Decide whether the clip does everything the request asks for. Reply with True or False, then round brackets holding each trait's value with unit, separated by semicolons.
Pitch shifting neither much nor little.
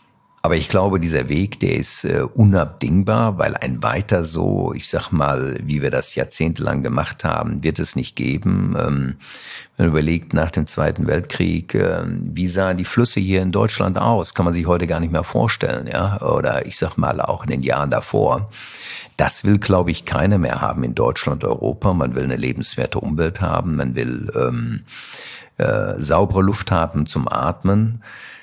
True (4.3 semitones)